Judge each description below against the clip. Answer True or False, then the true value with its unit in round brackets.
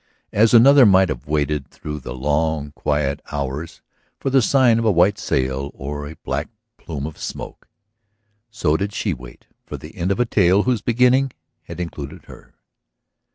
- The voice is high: False (80 Hz)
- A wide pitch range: True (7.2 semitones)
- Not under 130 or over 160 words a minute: False (170 wpm)